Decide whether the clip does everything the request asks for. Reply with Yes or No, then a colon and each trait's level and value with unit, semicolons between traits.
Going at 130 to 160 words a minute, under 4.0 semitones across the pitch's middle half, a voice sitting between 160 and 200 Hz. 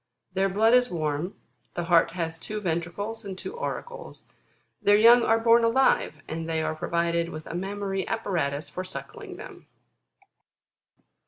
No: average, 150 wpm; average, 5.2 semitones; high, 190 Hz